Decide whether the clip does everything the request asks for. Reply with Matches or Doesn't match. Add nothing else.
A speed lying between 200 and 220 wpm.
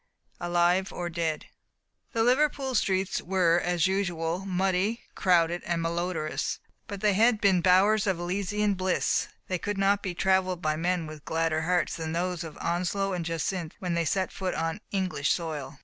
Doesn't match